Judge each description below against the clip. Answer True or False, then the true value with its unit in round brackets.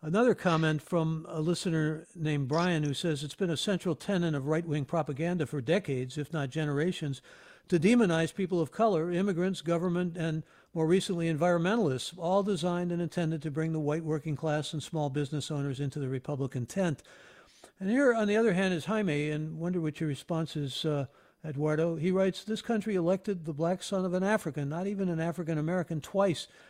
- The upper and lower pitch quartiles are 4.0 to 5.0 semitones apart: False (3.3 semitones)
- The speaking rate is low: False (190 wpm)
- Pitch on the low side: False (165 Hz)